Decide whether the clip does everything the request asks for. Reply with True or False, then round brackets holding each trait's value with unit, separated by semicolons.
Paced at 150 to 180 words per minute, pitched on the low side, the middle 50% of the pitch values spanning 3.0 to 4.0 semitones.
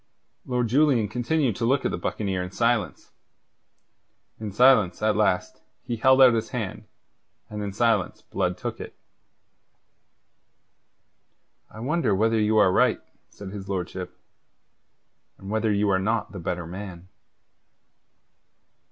False (135 wpm; 105 Hz; 3.5 semitones)